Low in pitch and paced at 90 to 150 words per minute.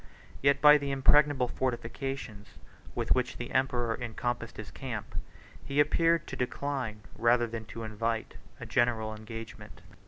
Yes: low, 120 Hz; slow, 135 wpm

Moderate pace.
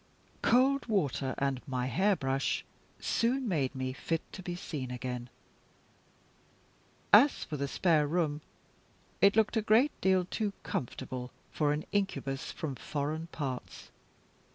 No: slow, 130 wpm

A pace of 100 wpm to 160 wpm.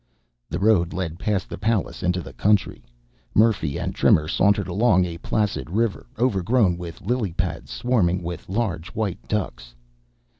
Yes: average, 150 wpm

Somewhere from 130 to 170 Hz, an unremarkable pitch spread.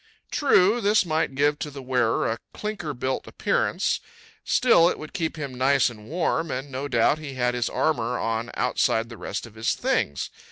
Yes: low, 135 Hz; average, 4.8 semitones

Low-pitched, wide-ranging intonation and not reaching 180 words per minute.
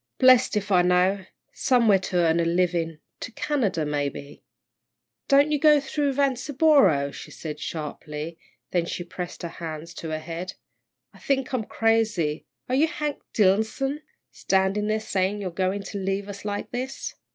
No: high, 195 Hz; wide, 7.1 semitones; average, 160 wpm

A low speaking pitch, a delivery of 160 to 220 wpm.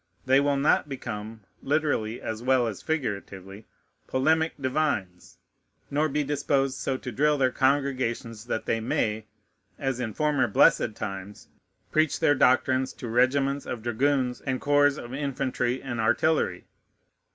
No: low, 130 Hz; average, 140 wpm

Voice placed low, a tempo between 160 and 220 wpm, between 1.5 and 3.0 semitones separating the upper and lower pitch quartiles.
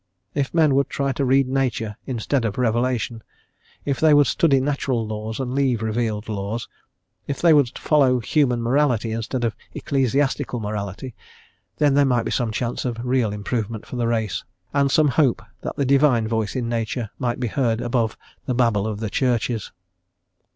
No: low, 125 Hz; average, 175 wpm; average, 3.4 semitones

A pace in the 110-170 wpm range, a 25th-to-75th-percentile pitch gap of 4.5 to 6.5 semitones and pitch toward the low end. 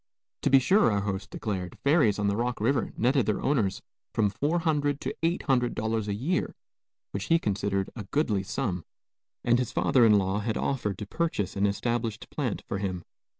No: average, 180 wpm; average, 5.3 semitones; low, 110 Hz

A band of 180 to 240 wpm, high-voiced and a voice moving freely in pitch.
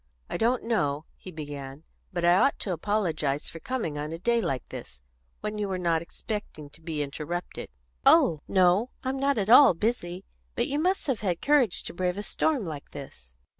No: average, 195 wpm; medium, 180 Hz; wide, 6.6 semitones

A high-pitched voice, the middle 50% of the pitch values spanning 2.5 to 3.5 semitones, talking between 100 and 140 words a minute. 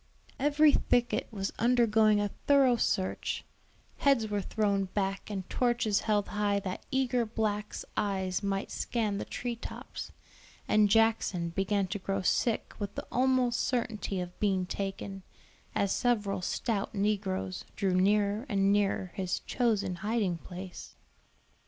Yes: high, 205 Hz; average, 2.9 semitones; slow, 135 wpm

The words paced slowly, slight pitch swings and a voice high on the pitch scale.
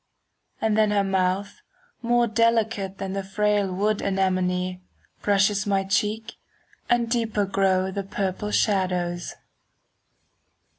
Yes: slow, 115 wpm; narrow, 2.1 semitones; high, 200 Hz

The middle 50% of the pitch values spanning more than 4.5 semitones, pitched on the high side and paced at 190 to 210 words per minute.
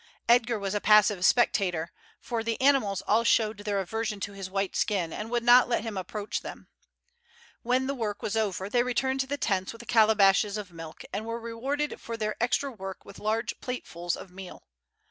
No: average, 3.2 semitones; high, 215 Hz; average, 200 wpm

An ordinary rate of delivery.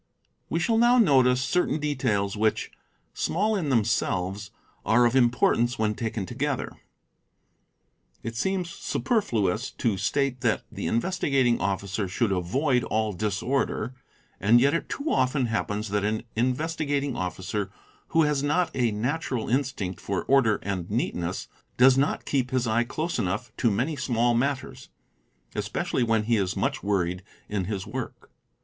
Yes: average, 145 wpm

